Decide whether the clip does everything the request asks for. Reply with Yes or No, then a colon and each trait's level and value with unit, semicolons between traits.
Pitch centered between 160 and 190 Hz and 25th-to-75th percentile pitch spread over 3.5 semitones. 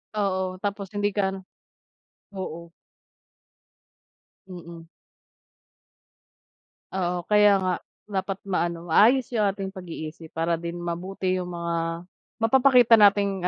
No: medium, 185 Hz; average, 3.0 semitones